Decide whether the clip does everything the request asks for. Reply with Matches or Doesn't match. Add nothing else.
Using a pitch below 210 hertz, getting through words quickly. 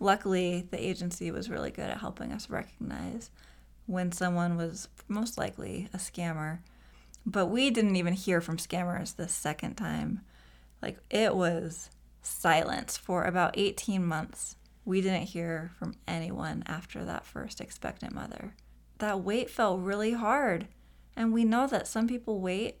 Doesn't match